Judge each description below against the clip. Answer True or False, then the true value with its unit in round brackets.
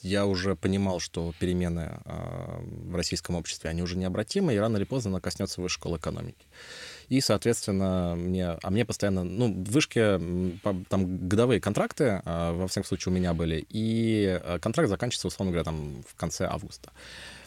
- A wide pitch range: False (3.1 semitones)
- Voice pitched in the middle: False (95 Hz)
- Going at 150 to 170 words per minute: True (160 wpm)